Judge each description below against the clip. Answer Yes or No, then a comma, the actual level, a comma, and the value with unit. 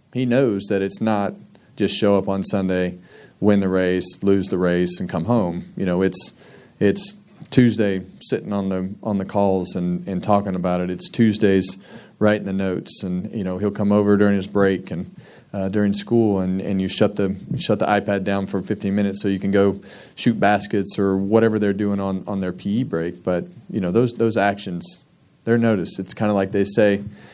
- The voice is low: Yes, low, 100 Hz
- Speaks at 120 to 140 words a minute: No, fast, 205 wpm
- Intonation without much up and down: Yes, narrow, 1.7 semitones